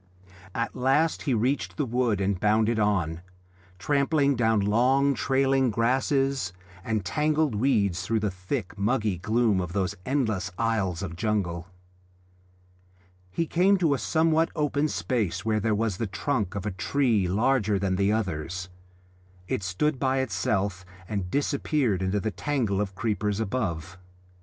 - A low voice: Yes, low, 110 Hz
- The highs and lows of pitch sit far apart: Yes, wide, 5.7 semitones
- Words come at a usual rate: Yes, average, 145 wpm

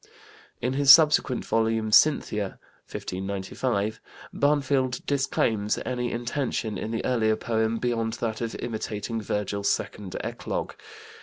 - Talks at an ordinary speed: No, slow, 110 wpm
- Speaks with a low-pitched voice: Yes, low, 115 Hz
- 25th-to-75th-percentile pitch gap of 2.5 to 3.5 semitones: Yes, average, 3.0 semitones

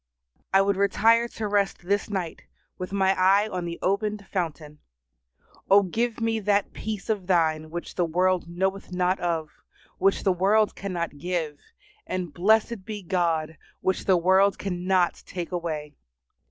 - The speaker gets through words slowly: No, average, 155 wpm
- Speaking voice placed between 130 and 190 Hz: Yes, medium, 185 Hz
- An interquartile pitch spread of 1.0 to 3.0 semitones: Yes, narrow, 2.6 semitones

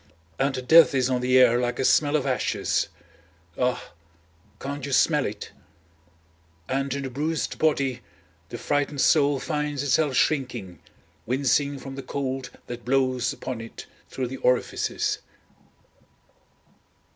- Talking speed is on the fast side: No, slow, 135 wpm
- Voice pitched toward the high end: No, low, 135 Hz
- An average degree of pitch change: No, narrow, 2.2 semitones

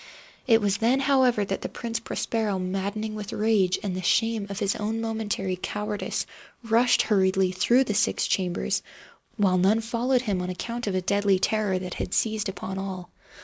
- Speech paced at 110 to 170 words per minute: No, average, 180 wpm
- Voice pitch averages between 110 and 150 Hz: No, high, 205 Hz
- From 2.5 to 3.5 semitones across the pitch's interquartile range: Yes, average, 2.9 semitones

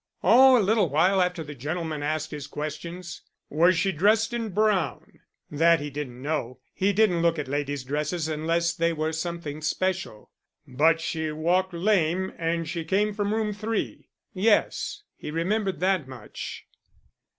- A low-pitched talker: No, medium, 170 Hz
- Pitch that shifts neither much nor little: Yes, average, 3.9 semitones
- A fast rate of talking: No, average, 155 wpm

